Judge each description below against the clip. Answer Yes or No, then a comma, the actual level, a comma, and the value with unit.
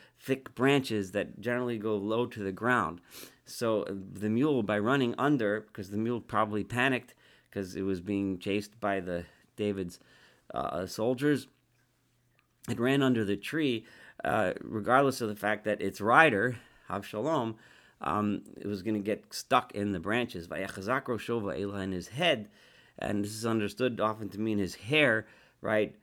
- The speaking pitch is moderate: No, low, 105 Hz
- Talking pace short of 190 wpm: Yes, average, 160 wpm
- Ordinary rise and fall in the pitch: Yes, average, 3.3 semitones